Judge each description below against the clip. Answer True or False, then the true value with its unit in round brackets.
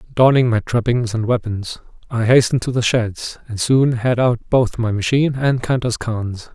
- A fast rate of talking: False (185 wpm)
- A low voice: True (120 Hz)